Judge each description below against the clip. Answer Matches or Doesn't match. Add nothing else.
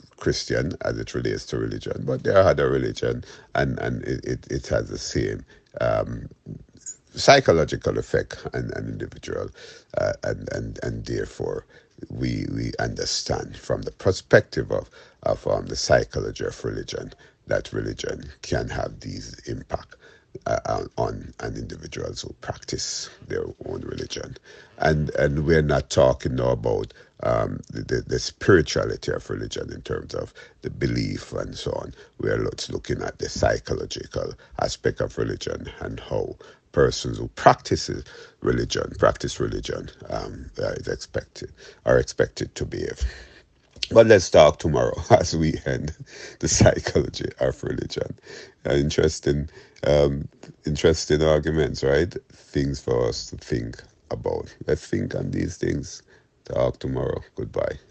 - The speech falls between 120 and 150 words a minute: Matches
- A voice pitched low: Matches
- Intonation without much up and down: Matches